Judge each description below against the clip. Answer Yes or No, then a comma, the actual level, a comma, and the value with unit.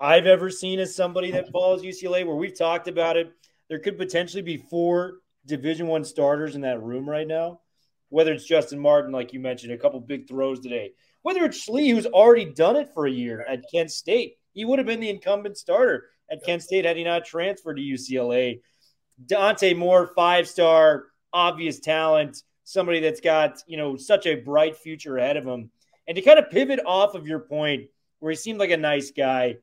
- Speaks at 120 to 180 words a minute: No, fast, 205 wpm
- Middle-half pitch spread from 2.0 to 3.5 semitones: No, average, 4.4 semitones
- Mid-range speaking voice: Yes, medium, 165 Hz